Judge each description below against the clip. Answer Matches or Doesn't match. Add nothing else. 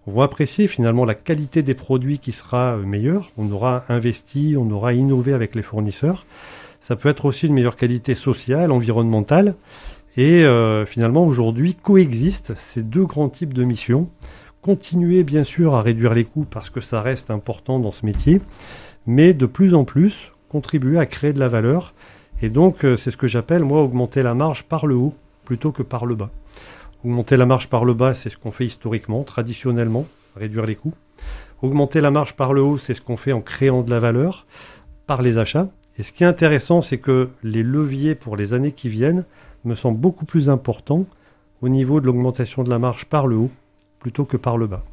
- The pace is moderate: Matches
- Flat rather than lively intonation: Doesn't match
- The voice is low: Matches